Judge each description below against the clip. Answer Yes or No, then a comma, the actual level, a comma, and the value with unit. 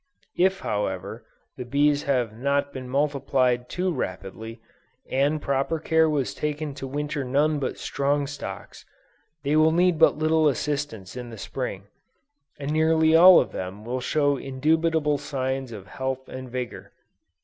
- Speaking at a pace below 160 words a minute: Yes, average, 150 wpm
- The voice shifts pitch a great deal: No, average, 3.3 semitones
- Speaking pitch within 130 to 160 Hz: Yes, medium, 140 Hz